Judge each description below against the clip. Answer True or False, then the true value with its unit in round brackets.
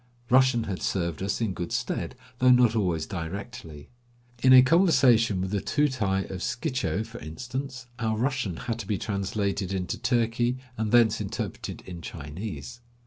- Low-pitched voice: True (110 Hz)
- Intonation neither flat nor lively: True (4.6 semitones)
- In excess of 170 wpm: False (155 wpm)